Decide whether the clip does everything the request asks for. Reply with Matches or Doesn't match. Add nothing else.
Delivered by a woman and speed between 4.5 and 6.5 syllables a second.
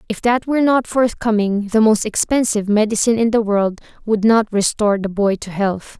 Matches